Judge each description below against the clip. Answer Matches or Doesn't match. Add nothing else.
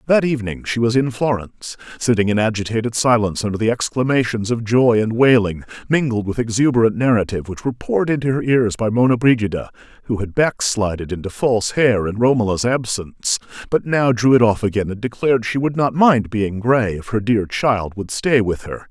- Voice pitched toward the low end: Matches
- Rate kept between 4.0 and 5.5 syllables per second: Doesn't match